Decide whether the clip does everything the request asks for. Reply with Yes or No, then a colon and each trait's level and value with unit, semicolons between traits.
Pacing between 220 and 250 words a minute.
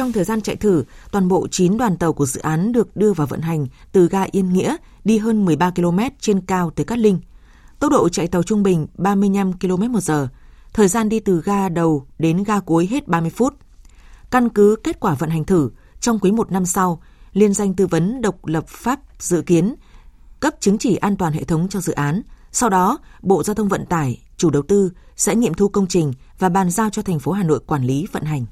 Yes: average, 230 wpm